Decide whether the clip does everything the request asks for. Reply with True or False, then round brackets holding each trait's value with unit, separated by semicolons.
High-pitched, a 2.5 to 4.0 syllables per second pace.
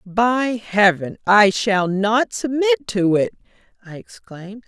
True (215 Hz; 3.8 syllables/s)